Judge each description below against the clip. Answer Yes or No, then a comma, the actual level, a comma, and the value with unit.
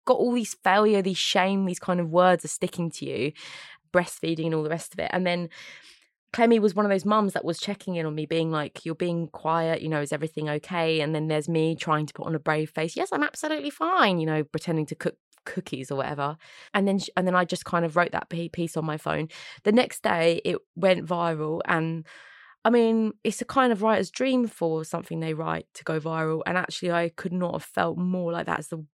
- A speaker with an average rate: No, fast, 240 wpm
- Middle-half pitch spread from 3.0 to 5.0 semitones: Yes, average, 3.5 semitones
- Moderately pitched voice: Yes, medium, 170 Hz